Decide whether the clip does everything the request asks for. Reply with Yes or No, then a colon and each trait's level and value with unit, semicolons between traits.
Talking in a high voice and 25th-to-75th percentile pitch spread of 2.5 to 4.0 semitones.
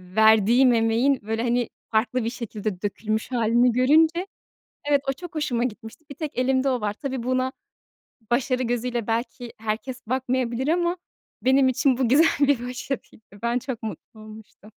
Yes: high, 245 Hz; average, 2.8 semitones